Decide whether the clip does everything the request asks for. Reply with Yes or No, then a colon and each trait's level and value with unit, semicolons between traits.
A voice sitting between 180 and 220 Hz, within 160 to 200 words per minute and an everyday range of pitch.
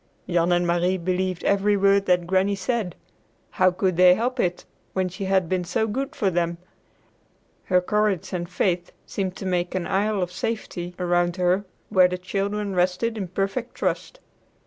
No: medium, 185 Hz; average, 170 wpm; narrow, 2.0 semitones